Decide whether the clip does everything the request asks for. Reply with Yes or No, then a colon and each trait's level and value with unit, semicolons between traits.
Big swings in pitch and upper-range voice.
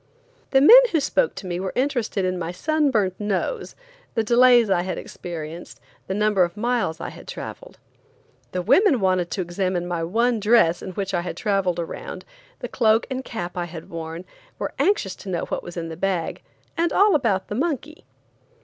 Yes: wide, 6.0 semitones; high, 195 Hz